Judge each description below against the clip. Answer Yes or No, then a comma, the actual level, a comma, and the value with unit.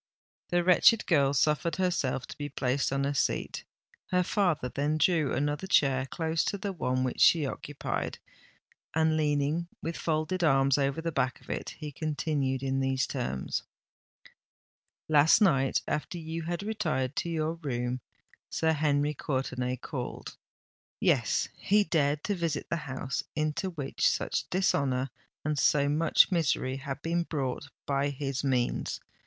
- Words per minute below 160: Yes, average, 140 wpm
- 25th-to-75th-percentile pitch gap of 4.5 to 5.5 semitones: No, average, 3.5 semitones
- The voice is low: No, medium, 145 Hz